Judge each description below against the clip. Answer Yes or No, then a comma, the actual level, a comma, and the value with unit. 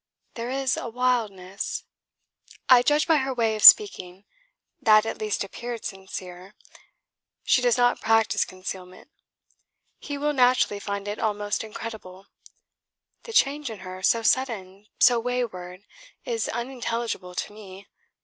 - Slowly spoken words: Yes, slow, 130 wpm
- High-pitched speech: Yes, high, 220 Hz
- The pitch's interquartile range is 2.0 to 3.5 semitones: No, average, 4.3 semitones